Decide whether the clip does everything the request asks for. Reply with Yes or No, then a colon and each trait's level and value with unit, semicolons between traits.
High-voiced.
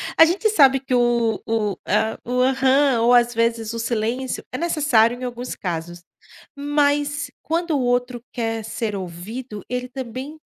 Yes: high, 245 Hz